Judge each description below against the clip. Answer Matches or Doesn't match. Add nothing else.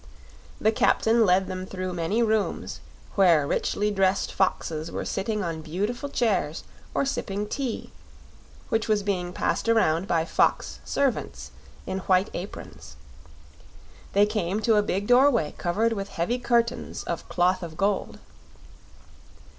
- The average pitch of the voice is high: Matches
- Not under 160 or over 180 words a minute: Doesn't match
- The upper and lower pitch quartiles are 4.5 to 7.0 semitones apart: Doesn't match